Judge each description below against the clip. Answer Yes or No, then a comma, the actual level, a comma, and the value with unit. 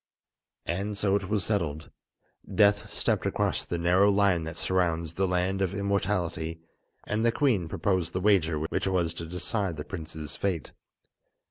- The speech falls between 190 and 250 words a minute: No, average, 155 wpm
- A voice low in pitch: Yes, very low, 90 Hz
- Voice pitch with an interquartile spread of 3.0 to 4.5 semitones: Yes, average, 3.3 semitones